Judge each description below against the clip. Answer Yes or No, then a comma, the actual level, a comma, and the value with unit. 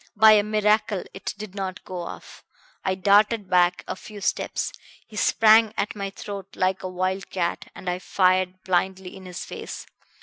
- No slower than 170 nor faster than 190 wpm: Yes, average, 175 wpm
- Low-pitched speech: No, high, 190 Hz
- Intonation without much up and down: Yes, narrow, 2.2 semitones